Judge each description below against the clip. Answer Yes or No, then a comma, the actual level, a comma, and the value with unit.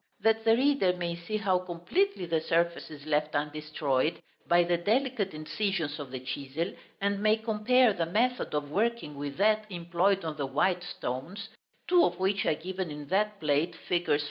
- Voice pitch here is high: No, medium, 175 Hz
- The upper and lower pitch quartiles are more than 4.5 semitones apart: Yes, wide, 5.5 semitones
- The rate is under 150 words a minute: No, average, 175 wpm